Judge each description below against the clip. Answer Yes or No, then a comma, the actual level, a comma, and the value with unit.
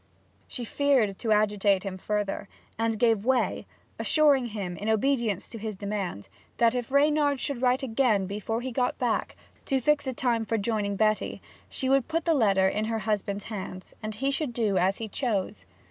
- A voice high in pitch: Yes, high, 225 Hz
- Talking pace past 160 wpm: Yes, average, 185 wpm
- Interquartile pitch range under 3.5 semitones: No, average, 4.1 semitones